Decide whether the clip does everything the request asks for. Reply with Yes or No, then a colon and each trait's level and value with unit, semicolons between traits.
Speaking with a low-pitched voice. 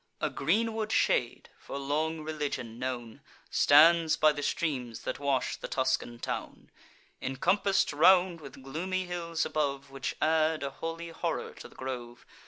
No: medium, 150 Hz